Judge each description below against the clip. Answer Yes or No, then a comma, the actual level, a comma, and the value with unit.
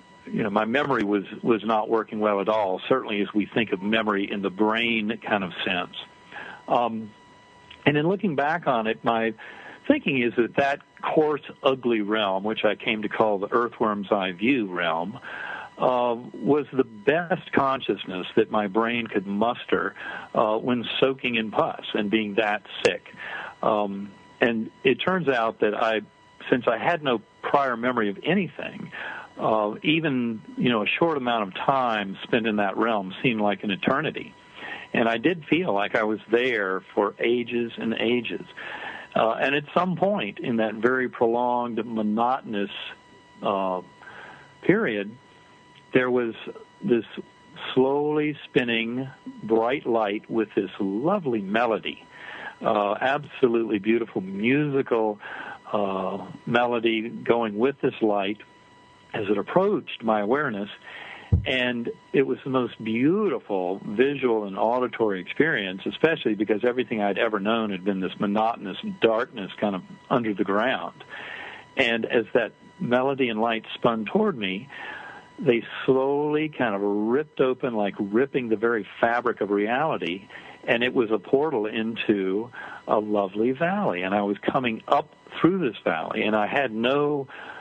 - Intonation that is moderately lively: Yes, average, 3.4 semitones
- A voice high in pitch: No, low, 115 Hz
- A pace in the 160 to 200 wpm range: No, average, 150 wpm